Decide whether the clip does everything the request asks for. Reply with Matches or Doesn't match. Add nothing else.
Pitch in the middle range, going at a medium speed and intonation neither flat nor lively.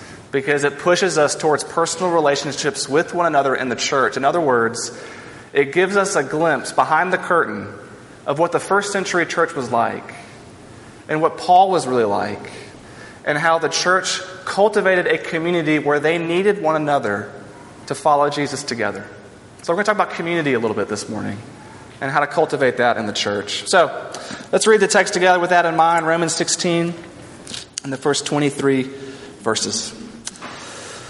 Matches